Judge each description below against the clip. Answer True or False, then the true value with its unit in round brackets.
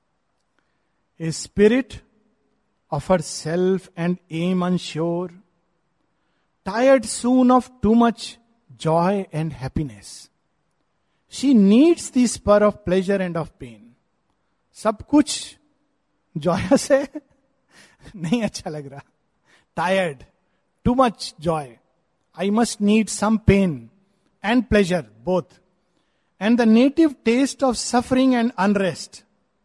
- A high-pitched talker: True (195 Hz)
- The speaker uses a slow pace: True (100 wpm)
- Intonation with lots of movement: True (5.7 semitones)